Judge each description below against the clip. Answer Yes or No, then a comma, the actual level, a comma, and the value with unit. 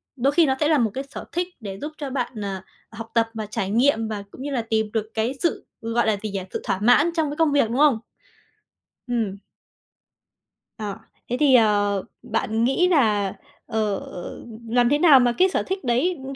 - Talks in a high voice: Yes, high, 235 Hz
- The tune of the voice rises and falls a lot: No, average, 4.6 semitones